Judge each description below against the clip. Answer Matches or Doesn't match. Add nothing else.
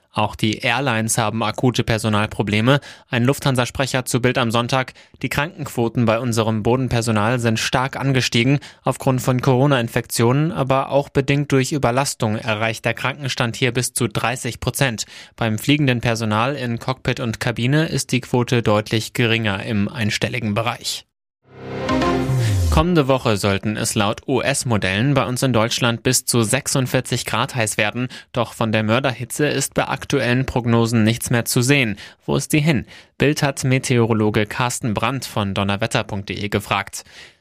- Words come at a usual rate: Matches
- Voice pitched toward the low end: Matches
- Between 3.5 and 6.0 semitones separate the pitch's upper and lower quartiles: Doesn't match